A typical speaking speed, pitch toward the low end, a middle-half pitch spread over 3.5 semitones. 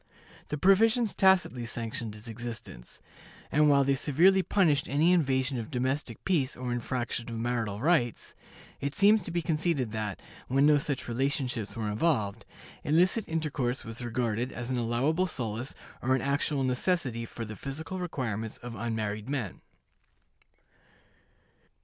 Yes: average, 145 wpm; low, 130 Hz; average, 5.0 semitones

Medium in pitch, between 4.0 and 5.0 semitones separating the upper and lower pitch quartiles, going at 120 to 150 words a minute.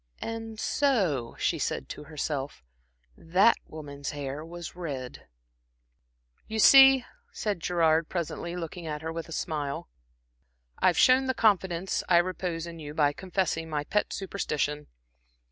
Yes: medium, 165 Hz; average, 4.3 semitones; slow, 135 wpm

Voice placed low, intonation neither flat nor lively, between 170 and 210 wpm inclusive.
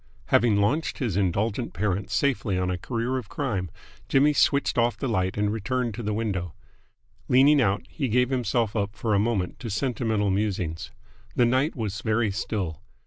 Yes: low, 110 Hz; average, 3.9 semitones; average, 175 wpm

